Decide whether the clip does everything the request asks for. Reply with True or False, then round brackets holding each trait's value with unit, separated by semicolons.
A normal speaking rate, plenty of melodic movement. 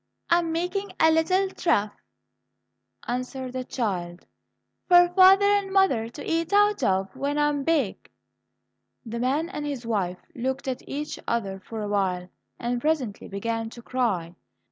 True (155 wpm; 6.9 semitones)